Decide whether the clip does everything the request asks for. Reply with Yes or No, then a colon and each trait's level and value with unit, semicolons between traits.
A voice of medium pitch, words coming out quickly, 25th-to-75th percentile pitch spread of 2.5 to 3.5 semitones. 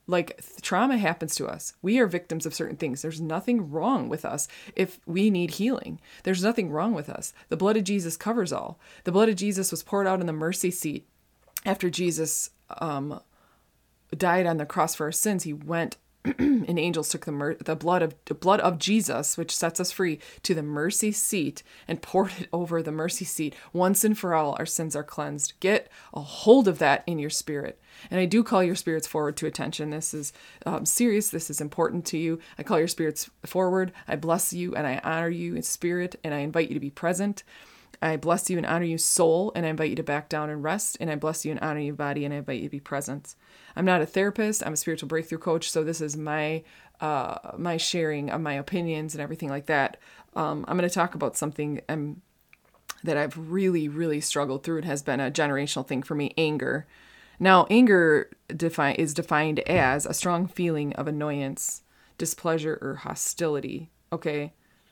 Yes: medium, 165 Hz; fast, 210 wpm; average, 3.2 semitones